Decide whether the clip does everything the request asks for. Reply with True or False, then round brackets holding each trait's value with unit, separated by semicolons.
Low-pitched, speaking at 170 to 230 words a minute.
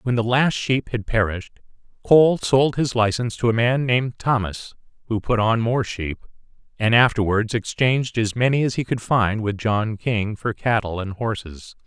True (115 Hz; 180 wpm)